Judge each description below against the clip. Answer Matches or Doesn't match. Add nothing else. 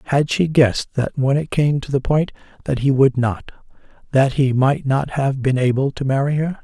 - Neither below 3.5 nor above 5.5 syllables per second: Matches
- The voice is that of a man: Matches